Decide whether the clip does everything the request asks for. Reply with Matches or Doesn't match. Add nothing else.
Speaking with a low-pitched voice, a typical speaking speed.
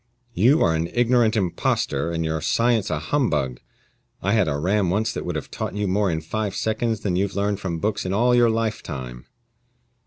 Matches